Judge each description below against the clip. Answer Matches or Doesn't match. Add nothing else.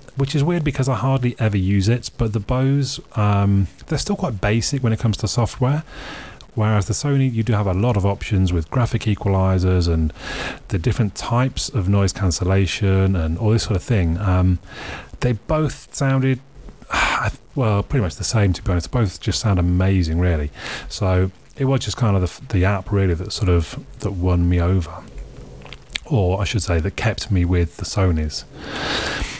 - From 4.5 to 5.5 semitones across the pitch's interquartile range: Matches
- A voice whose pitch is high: Doesn't match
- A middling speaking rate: Matches